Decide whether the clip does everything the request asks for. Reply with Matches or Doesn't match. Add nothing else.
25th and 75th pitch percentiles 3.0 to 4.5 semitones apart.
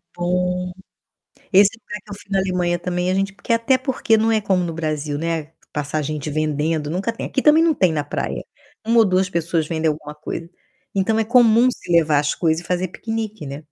Doesn't match